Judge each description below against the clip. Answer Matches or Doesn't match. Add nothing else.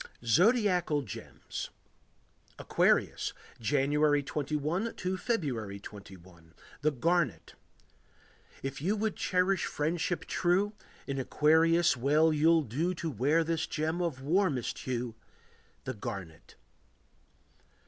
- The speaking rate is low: Matches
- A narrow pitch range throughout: Doesn't match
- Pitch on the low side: Doesn't match